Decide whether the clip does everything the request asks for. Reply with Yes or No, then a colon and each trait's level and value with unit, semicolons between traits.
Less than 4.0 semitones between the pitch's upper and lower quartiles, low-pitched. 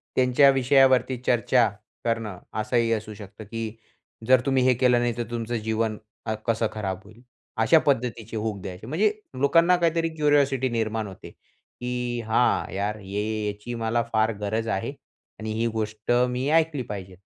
Yes: average, 3.1 semitones; low, 115 Hz